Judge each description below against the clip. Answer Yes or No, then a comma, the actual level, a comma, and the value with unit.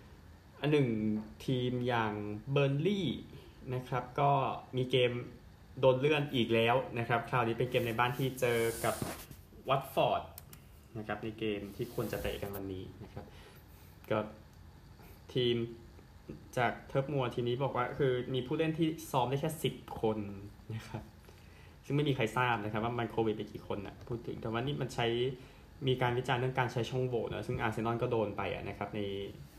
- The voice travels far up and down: No, average, 3.4 semitones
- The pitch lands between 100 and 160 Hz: Yes, low, 120 Hz